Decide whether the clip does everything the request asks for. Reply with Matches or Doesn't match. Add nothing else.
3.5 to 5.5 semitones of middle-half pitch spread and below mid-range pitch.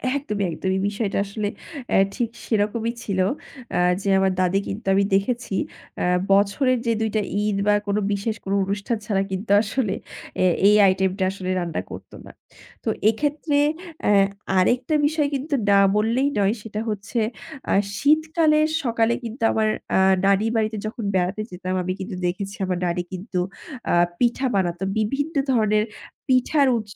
Doesn't match